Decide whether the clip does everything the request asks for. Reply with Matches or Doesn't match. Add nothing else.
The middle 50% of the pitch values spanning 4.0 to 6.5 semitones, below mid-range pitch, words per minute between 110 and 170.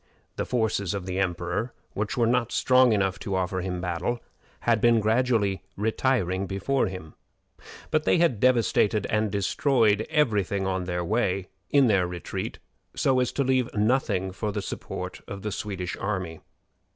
Matches